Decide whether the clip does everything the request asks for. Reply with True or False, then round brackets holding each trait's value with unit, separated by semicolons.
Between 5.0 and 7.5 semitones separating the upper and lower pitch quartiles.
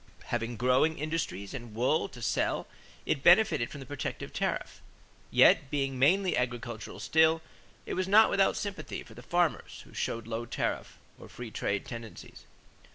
True (5.4 semitones)